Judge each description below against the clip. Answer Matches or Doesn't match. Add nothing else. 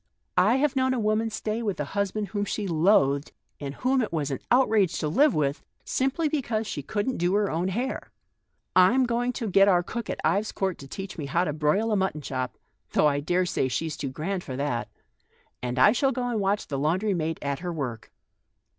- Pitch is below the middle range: Doesn't match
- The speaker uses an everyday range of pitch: Doesn't match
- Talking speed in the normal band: Doesn't match